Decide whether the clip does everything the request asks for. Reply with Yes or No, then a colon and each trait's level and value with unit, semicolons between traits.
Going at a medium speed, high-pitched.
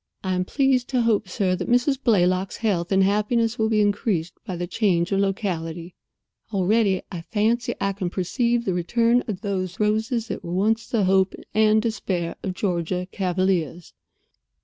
Yes: average, 170 wpm; high, 195 Hz